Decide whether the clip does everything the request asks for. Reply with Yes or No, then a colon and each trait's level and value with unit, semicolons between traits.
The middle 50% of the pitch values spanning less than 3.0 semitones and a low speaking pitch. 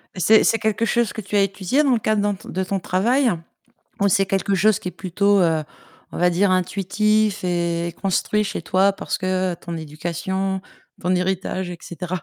No: narrow, 2.4 semitones; high, 190 Hz